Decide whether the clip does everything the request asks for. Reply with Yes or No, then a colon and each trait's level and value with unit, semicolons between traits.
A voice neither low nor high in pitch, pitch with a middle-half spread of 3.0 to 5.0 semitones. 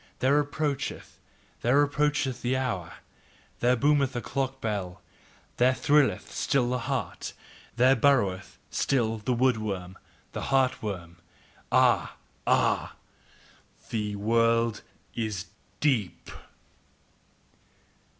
No: low, 125 Hz; average, 4.0 semitones